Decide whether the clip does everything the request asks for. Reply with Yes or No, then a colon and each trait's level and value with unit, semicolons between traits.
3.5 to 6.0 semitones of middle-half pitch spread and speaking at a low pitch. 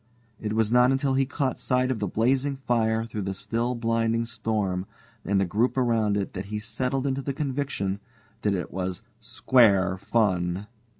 Yes: average, 4.2 semitones; low, 115 Hz